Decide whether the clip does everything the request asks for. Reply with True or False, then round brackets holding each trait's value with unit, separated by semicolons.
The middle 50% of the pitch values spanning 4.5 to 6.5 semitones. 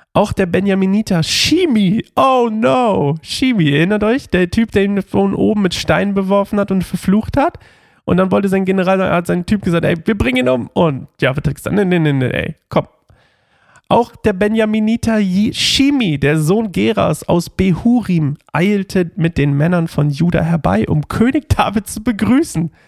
True (4.9 semitones)